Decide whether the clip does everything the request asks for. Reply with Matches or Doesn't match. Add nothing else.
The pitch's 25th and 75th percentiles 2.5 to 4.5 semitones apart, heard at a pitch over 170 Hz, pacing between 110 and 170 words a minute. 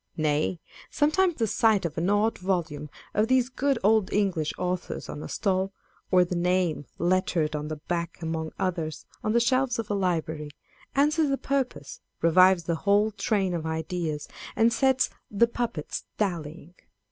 Doesn't match